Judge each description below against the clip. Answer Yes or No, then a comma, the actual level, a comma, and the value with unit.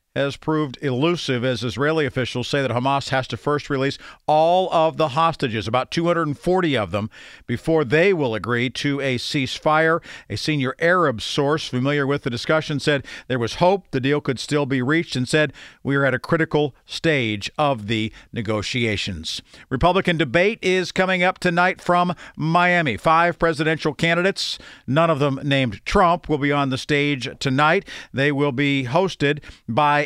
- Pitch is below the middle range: No, medium, 145 Hz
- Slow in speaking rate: No, average, 170 wpm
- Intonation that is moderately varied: Yes, average, 4.0 semitones